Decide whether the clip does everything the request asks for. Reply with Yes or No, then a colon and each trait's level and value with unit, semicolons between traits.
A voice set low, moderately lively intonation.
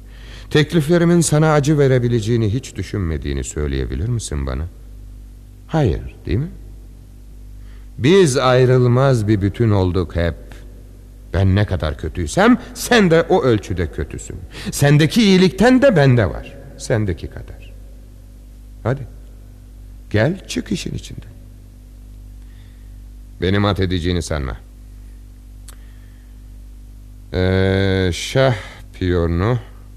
Yes: low, 105 Hz; average, 5.0 semitones